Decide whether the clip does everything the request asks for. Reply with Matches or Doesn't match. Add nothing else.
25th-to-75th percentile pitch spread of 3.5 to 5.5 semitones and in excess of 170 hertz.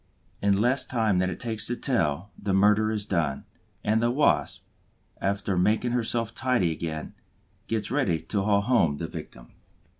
Doesn't match